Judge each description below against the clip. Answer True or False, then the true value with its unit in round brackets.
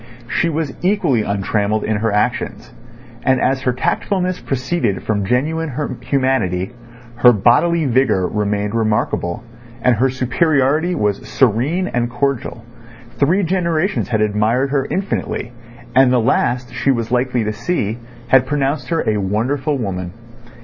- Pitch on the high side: False (125 Hz)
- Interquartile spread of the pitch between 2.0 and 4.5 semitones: False (5.0 semitones)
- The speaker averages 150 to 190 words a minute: False (135 wpm)